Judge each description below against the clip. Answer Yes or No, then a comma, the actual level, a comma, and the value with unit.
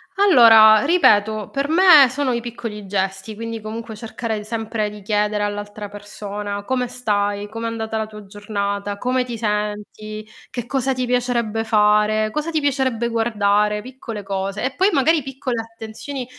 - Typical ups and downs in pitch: Yes, average, 3.1 semitones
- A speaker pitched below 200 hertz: No, high, 220 Hz